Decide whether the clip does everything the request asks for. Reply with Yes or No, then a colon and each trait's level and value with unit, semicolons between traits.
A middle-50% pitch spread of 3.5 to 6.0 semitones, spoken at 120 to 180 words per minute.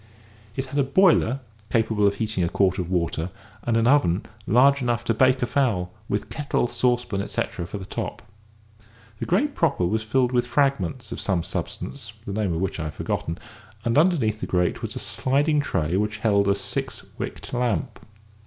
No: wide, 5.4 semitones; average, 190 wpm